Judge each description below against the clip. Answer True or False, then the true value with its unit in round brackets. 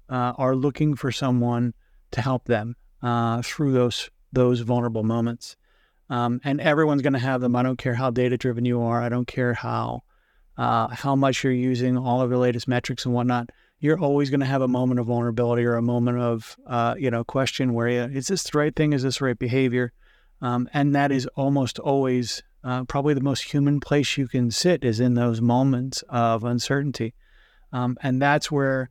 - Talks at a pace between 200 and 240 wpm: True (205 wpm)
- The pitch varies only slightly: True (2.1 semitones)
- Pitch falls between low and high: False (125 Hz)